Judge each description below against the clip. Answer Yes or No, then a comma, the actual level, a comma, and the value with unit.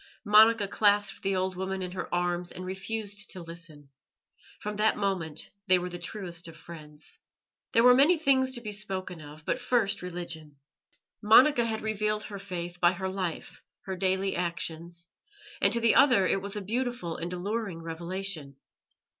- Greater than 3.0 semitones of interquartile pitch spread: Yes, average, 3.6 semitones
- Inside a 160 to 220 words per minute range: Yes, average, 170 wpm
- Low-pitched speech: No, high, 190 Hz